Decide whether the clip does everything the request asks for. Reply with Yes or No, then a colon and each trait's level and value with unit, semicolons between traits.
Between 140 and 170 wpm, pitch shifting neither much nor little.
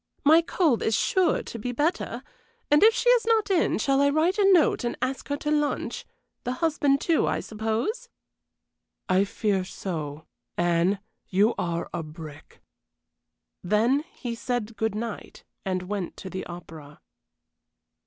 No: average, 155 wpm; wide, 8.3 semitones